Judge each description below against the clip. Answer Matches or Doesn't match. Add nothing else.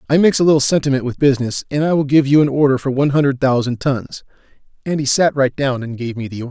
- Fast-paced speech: Matches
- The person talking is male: Matches